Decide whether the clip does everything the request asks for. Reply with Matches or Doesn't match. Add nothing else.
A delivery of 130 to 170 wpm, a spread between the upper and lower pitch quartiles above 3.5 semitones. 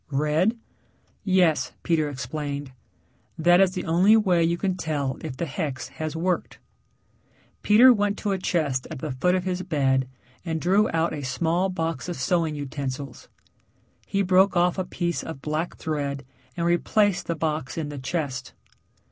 Matches